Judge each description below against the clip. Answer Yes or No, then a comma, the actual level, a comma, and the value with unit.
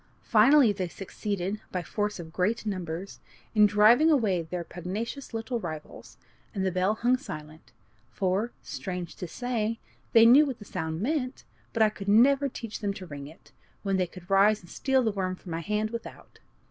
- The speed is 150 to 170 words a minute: No, average, 185 wpm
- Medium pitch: No, high, 205 Hz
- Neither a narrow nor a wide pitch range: Yes, average, 4.2 semitones